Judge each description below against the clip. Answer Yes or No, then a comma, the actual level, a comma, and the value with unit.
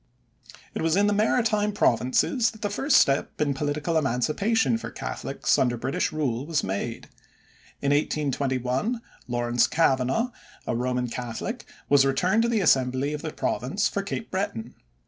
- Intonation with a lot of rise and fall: Yes, wide, 8.3 semitones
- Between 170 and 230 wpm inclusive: No, average, 150 wpm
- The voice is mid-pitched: Yes, medium, 145 Hz